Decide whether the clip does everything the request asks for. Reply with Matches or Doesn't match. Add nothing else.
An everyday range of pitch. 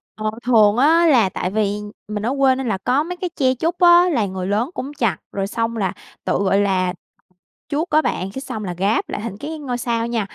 Doesn't match